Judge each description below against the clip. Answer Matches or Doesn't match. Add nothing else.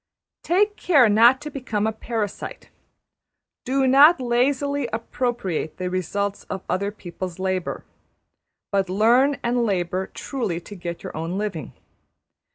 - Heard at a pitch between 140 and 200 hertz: Doesn't match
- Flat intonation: Doesn't match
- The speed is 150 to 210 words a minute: Doesn't match